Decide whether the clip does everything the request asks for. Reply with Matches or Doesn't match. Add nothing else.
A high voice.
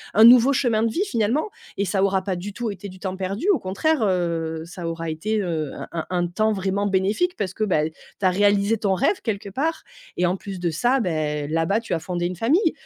Matches